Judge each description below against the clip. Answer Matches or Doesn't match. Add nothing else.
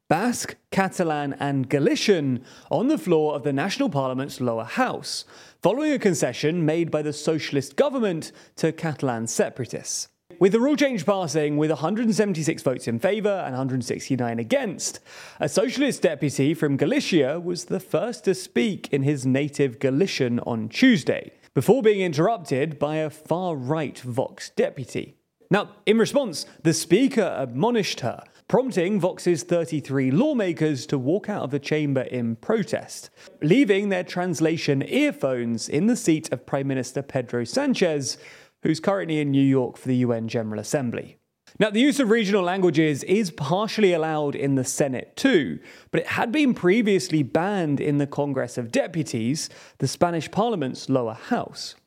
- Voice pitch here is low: Doesn't match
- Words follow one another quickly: Doesn't match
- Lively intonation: Matches